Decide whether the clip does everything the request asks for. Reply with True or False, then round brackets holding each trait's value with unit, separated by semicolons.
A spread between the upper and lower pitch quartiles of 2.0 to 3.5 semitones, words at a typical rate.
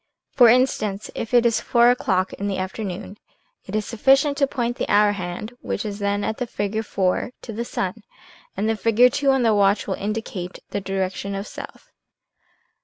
True (3.2 semitones; 190 wpm)